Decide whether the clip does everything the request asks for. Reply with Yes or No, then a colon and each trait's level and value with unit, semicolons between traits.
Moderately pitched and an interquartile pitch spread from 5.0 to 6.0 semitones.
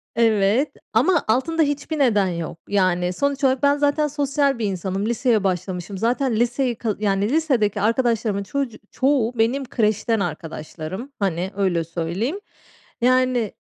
No: high, 225 Hz; wide, 5.6 semitones